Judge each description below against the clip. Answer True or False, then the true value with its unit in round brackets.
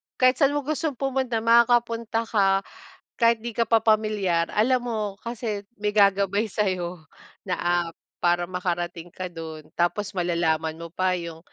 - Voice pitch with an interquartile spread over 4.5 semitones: True (4.9 semitones)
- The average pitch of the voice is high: True (205 Hz)